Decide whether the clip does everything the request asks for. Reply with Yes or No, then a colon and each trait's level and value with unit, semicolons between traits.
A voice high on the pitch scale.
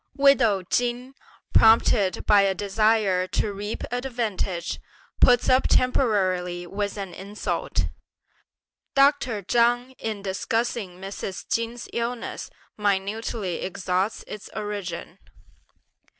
Yes: high, 210 Hz